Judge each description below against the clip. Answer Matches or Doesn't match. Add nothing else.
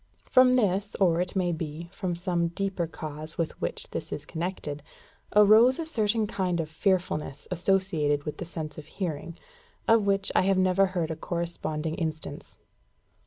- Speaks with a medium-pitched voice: Matches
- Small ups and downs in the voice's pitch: Doesn't match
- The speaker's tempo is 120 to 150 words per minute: Doesn't match